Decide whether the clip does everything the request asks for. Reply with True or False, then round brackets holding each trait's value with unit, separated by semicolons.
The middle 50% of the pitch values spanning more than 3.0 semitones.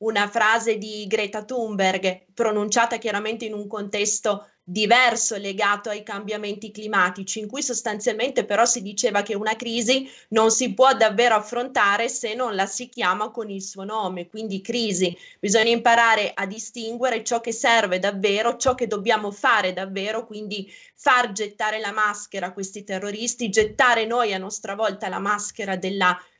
False (2.4 semitones)